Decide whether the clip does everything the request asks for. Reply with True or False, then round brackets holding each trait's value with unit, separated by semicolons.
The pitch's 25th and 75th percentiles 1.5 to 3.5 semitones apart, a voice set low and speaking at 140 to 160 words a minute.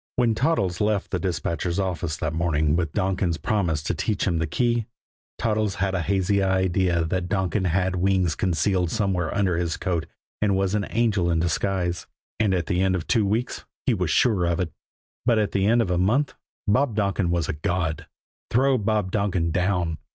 False (3.1 semitones; 95 Hz; 190 wpm)